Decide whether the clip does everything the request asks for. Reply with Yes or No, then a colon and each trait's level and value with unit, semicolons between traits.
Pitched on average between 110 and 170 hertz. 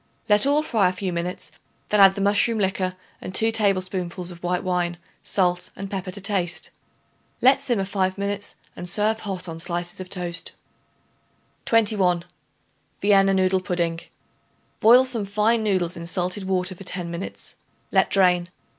No: high, 190 Hz